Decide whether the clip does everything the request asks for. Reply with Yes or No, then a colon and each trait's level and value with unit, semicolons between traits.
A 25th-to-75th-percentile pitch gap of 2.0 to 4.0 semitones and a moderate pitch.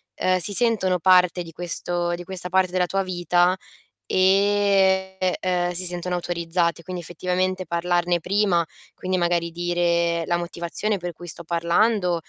No: narrow, 1.4 semitones; medium, 180 Hz